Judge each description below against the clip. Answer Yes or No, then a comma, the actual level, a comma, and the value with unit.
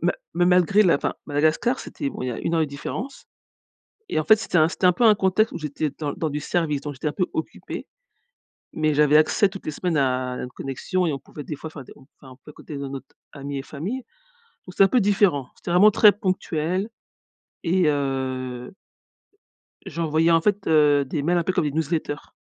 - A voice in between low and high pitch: Yes, medium, 155 Hz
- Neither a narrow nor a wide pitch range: Yes, average, 4.4 semitones